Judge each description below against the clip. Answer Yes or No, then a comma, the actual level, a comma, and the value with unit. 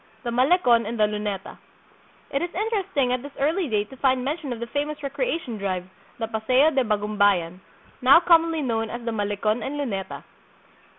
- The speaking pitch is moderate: No, high, 245 Hz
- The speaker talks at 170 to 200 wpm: Yes, average, 175 wpm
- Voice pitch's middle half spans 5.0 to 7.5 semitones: Yes, wide, 5.4 semitones